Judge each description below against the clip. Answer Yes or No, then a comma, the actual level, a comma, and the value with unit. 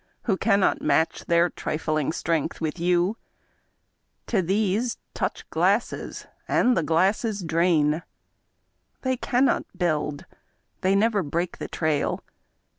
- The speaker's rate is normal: No, slow, 115 wpm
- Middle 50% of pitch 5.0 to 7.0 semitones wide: No, average, 4.1 semitones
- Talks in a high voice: No, medium, 175 Hz